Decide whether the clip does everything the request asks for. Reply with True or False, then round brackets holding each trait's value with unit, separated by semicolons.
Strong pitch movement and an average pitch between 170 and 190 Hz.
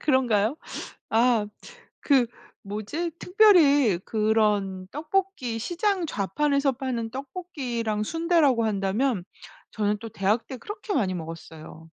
False (6.2 semitones; 240 Hz)